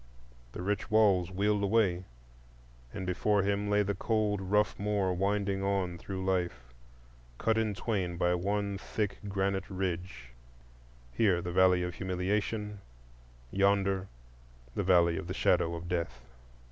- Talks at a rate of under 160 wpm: Yes, slow, 135 wpm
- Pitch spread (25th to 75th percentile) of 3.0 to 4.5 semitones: No, narrow, 2.5 semitones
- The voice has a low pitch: Yes, very low, 95 Hz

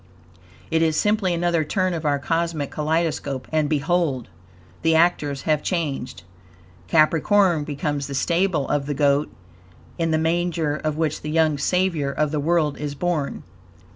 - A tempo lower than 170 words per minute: Yes, average, 150 wpm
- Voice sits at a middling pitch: Yes, medium, 155 Hz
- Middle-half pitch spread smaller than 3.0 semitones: Yes, narrow, 2.6 semitones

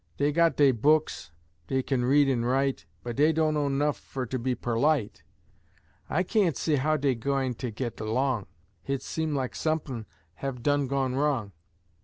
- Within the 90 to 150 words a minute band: No, average, 165 wpm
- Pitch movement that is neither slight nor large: Yes, average, 3.0 semitones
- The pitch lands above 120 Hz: Yes, low, 135 Hz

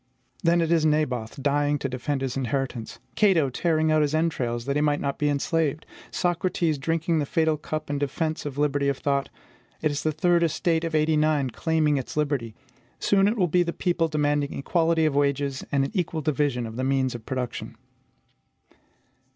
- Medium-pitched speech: Yes, medium, 150 Hz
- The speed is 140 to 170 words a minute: No, average, 185 wpm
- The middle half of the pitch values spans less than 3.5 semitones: Yes, average, 2.8 semitones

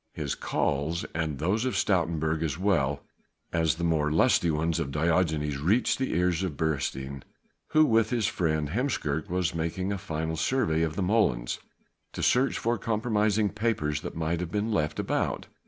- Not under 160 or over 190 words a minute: Yes, average, 170 wpm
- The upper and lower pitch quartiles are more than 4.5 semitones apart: Yes, average, 5.0 semitones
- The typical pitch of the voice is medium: No, very low, 85 Hz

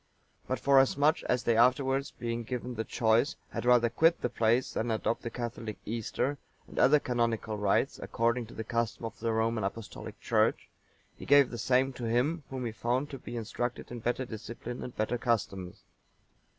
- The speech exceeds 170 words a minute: Yes, average, 180 wpm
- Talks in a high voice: No, low, 120 Hz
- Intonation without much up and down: Yes, narrow, 2.1 semitones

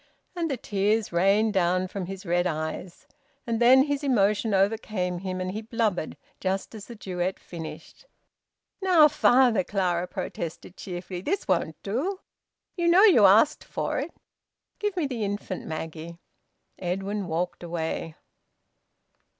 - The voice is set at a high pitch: Yes, high, 195 Hz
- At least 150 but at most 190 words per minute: No, average, 140 wpm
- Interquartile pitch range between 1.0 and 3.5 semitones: No, average, 4.8 semitones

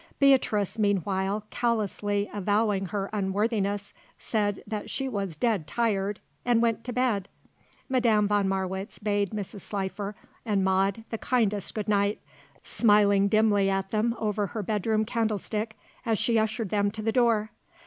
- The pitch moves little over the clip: Yes, narrow, 1.9 semitones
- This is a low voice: No, high, 210 Hz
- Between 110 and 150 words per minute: Yes, average, 145 wpm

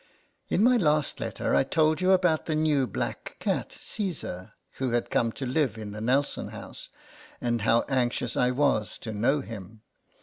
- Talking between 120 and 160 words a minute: No, average, 175 wpm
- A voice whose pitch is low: Yes, low, 130 Hz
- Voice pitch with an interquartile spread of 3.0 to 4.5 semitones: No, average, 5.2 semitones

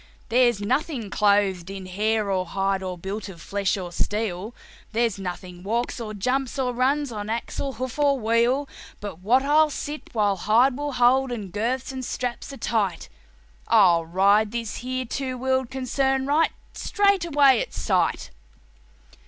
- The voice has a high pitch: Yes, high, 230 Hz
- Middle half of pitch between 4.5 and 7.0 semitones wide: Yes, average, 4.9 semitones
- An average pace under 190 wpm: Yes, average, 160 wpm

